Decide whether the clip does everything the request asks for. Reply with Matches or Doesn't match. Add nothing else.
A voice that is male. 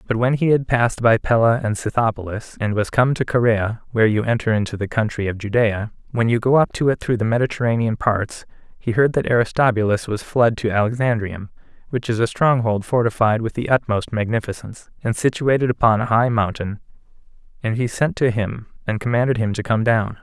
Matches